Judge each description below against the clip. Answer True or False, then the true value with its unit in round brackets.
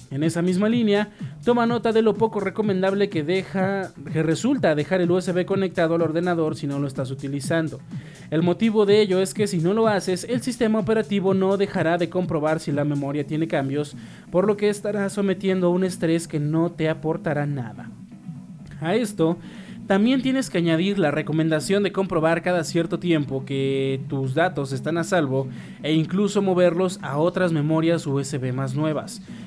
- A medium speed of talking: True (180 wpm)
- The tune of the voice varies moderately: True (4.0 semitones)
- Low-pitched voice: False (175 Hz)